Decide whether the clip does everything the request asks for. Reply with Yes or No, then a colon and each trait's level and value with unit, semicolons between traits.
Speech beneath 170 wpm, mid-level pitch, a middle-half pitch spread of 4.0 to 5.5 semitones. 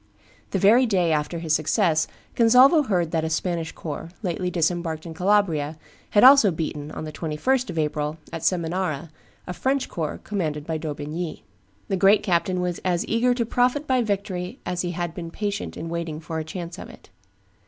No: average, 185 wpm; medium, 175 Hz; average, 4.3 semitones